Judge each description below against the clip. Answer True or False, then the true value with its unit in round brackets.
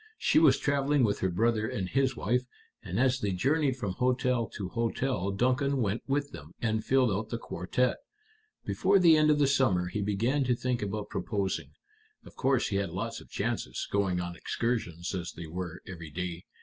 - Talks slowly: False (190 wpm)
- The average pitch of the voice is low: True (115 Hz)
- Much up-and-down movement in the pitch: True (5.8 semitones)